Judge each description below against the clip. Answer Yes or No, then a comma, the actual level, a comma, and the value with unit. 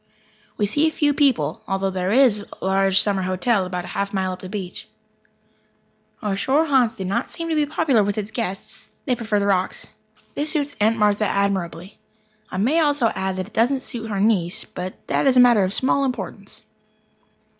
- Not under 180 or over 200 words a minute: Yes, average, 190 wpm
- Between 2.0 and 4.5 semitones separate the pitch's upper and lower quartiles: No, average, 5.2 semitones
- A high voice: Yes, high, 210 Hz